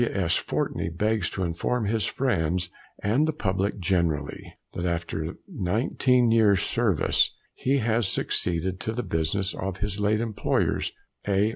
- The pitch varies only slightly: No, average, 4.3 semitones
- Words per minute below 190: Yes, average, 145 wpm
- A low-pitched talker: Yes, low, 100 Hz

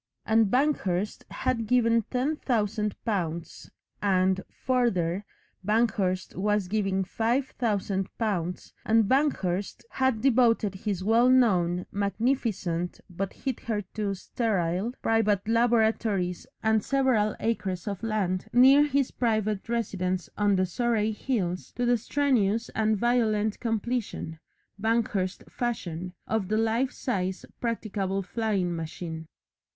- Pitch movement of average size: Yes, average, 3.8 semitones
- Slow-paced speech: Yes, slow, 115 wpm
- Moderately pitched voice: No, high, 215 Hz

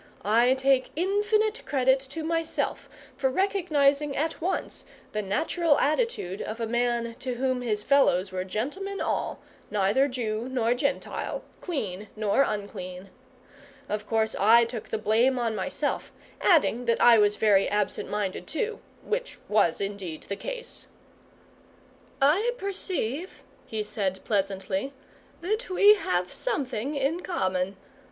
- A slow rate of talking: Yes, slow, 130 wpm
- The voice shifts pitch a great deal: Yes, wide, 7.4 semitones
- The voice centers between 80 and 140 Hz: No, high, 245 Hz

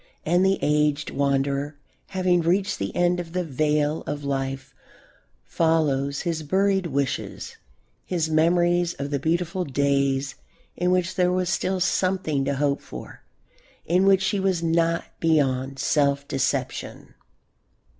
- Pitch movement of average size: Yes, average, 4.1 semitones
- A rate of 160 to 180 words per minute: No, slow, 135 wpm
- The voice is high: No, medium, 160 Hz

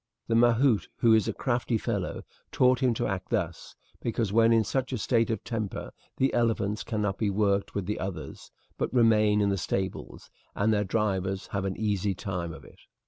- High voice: No, low, 105 Hz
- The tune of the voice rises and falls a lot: No, average, 2.8 semitones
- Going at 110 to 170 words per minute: No, average, 195 wpm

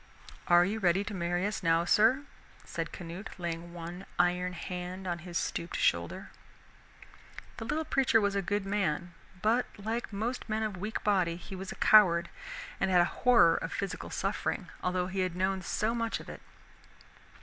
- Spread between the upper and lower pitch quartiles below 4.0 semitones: Yes, average, 3.3 semitones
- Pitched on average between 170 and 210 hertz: Yes, medium, 185 Hz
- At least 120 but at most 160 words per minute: No, average, 175 wpm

